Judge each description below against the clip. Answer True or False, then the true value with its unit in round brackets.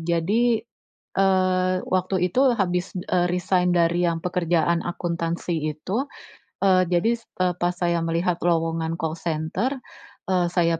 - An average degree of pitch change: False (1.7 semitones)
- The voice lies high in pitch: False (175 Hz)